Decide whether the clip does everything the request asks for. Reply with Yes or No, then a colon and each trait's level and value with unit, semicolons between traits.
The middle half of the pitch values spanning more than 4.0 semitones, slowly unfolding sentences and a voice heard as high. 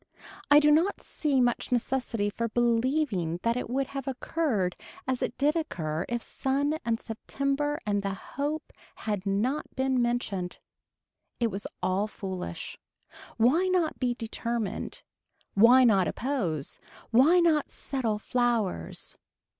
Yes: average, 5.0 semitones; slow, 130 wpm; high, 240 Hz